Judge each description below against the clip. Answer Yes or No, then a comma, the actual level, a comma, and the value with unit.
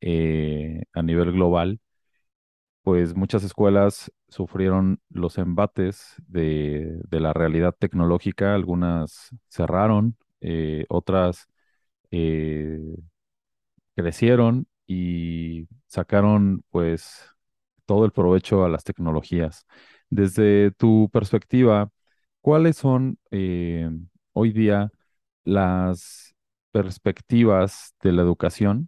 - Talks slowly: Yes, slow, 90 wpm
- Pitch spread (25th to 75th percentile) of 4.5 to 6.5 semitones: No, average, 3.6 semitones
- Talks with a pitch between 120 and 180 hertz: No, very low, 95 Hz